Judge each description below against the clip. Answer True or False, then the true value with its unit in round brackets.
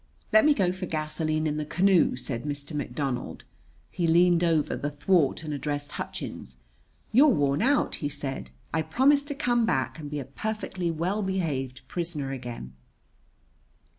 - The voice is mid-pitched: True (155 Hz)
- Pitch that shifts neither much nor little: True (4.7 semitones)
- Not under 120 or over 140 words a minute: False (160 wpm)